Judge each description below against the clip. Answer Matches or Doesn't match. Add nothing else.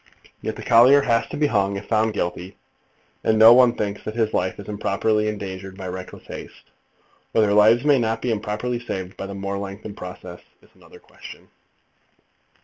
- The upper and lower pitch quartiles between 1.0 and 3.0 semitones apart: Matches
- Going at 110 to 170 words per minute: Doesn't match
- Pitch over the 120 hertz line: Doesn't match